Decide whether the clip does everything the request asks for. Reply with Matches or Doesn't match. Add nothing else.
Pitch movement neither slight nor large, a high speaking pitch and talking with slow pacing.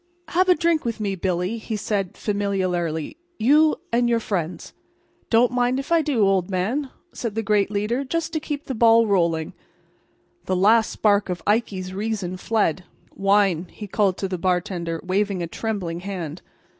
Doesn't match